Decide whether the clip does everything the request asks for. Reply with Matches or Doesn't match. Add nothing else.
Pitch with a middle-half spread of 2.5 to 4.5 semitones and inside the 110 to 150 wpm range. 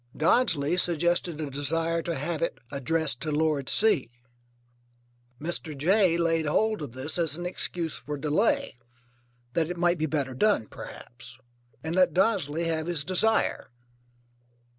Matches